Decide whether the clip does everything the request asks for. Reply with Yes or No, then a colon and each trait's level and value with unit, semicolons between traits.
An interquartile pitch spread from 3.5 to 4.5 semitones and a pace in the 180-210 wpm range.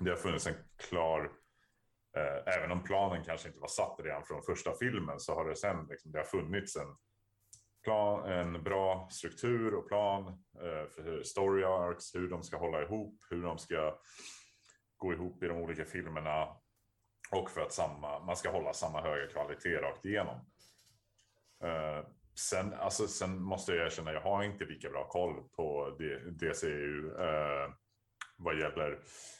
No: average, 4.1 semitones; average, 165 wpm